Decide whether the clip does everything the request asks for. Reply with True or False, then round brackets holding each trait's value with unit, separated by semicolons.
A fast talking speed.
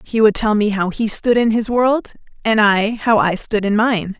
True (245 wpm)